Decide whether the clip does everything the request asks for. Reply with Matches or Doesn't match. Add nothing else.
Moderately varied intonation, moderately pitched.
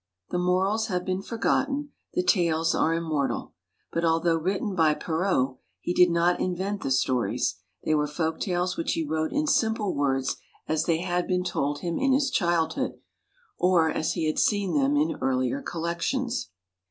Matches